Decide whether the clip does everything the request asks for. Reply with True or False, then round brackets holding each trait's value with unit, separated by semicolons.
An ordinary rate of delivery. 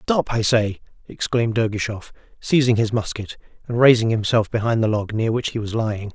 True (185 wpm)